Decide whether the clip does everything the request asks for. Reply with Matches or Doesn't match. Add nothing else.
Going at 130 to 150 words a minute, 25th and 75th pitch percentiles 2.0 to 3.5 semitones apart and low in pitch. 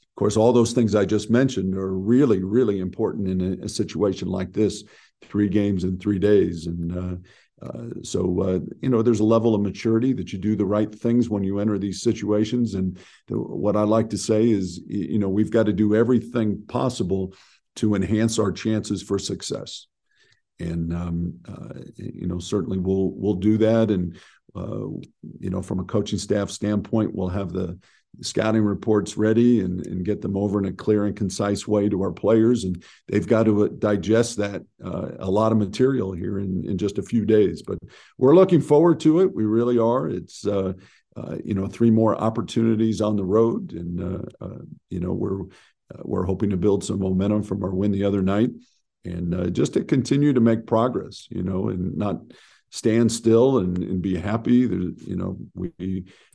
Doesn't match